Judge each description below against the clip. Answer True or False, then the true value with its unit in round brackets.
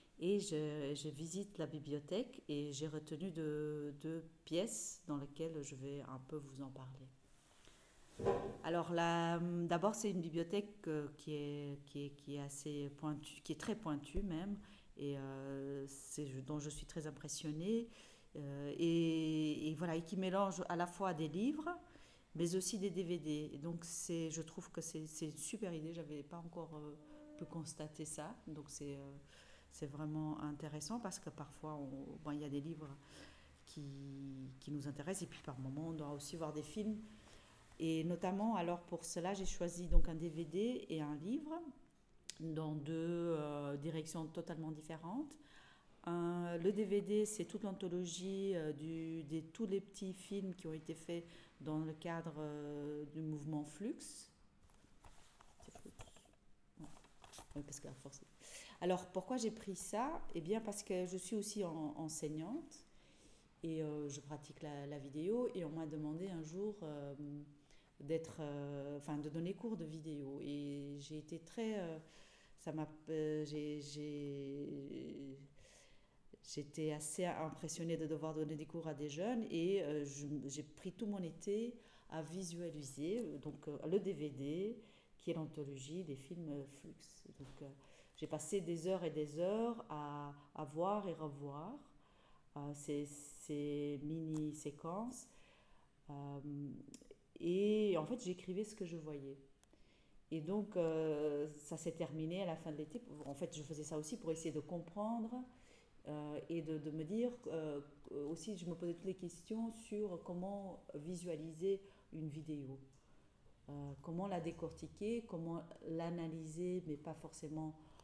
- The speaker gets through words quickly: False (160 wpm)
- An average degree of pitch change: True (3.6 semitones)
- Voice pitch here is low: False (160 Hz)